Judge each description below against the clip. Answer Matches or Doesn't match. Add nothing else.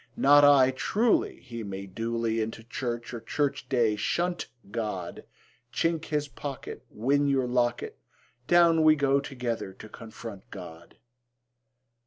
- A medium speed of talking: Doesn't match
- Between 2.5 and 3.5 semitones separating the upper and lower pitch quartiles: Doesn't match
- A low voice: Matches